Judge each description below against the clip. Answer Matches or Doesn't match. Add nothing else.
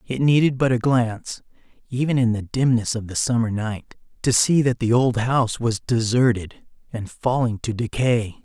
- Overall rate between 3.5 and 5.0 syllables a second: Matches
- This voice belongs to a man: Matches